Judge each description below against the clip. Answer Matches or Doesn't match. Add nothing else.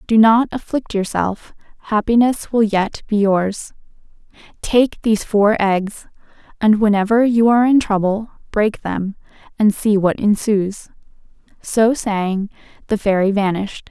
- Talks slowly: Matches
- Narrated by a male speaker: Doesn't match